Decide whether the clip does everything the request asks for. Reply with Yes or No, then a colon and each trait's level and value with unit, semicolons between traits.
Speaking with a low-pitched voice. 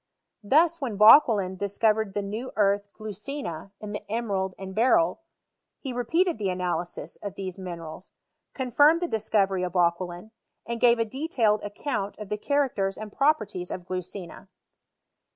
No: high, 210 Hz